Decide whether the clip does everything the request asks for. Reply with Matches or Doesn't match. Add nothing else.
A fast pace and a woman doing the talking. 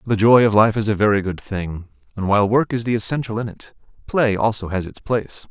Doesn't match